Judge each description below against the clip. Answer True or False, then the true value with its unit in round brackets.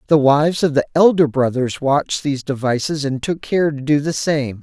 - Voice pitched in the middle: True (145 Hz)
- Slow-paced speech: False (205 wpm)